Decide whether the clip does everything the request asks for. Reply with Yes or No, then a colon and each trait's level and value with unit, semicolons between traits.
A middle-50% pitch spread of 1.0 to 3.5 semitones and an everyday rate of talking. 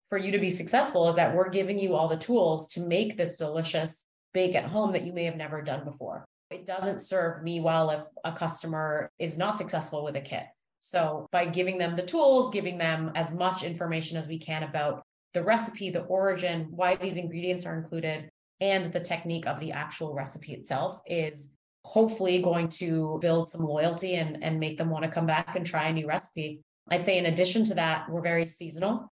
No: narrow, 2.5 semitones; fast, 210 wpm